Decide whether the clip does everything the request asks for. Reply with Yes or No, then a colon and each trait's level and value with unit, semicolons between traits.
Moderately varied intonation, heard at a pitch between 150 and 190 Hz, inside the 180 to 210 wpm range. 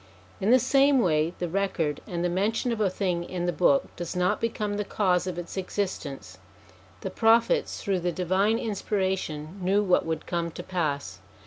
Yes: average, 3.3 semitones; medium, 185 Hz; average, 190 wpm